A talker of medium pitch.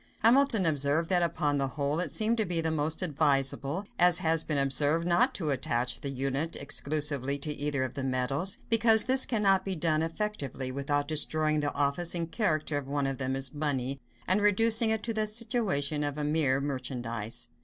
Yes: medium, 150 Hz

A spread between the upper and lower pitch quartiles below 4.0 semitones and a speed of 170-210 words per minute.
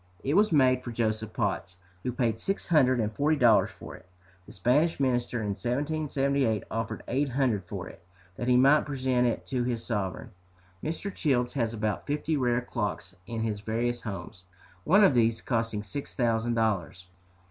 Yes: average, 3.6 semitones; average, 175 wpm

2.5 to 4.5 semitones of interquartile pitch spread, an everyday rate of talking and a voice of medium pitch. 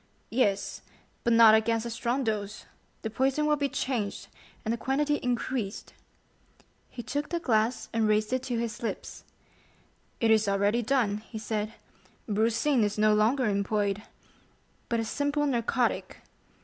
No: average, 3.2 semitones; average, 150 wpm; high, 230 Hz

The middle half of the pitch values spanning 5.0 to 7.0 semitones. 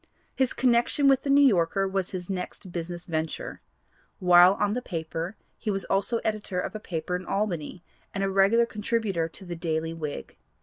No: average, 3.8 semitones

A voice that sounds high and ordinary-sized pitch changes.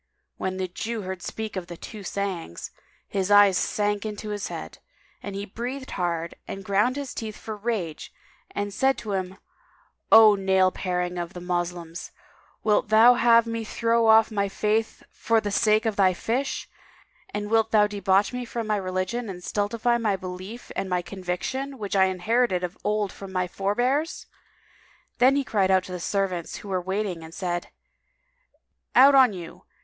Yes: high, 205 Hz; average, 3.3 semitones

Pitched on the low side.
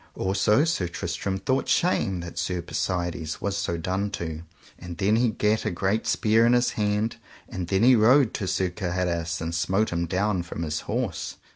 Yes: very low, 95 Hz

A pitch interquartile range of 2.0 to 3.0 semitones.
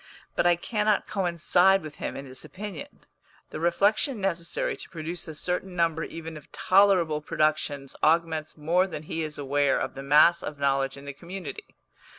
No: average, 3.5 semitones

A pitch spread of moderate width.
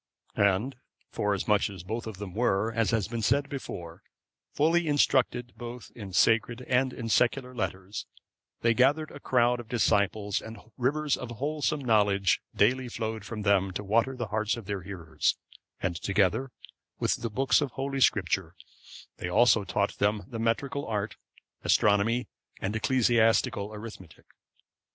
Yes: average, 3.7 semitones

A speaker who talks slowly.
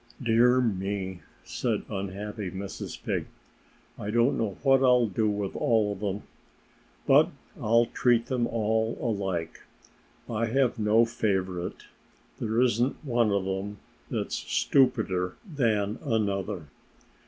Yes: slow, 120 wpm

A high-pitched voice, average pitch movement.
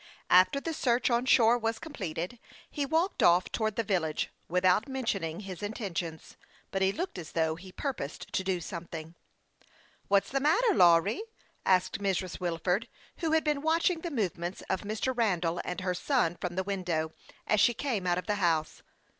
No: high, 195 Hz; wide, 5.8 semitones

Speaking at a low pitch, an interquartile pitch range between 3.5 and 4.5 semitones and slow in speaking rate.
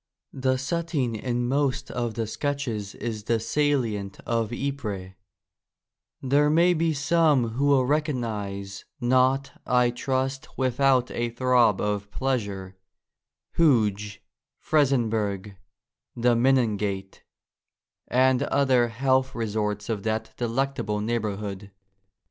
Yes: low, 120 Hz; average, 4.2 semitones; slow, 115 wpm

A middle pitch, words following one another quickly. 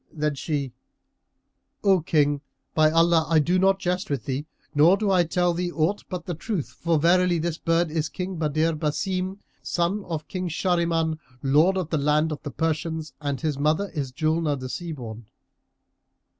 No: medium, 160 Hz; average, 175 wpm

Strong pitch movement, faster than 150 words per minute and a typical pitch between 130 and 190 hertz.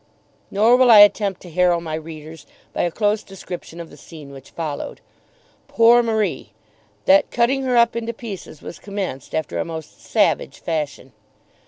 Yes: wide, 6.2 semitones; average, 165 wpm; medium, 185 Hz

